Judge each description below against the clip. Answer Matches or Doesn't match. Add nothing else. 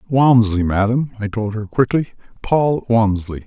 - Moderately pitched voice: Doesn't match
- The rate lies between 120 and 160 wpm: Matches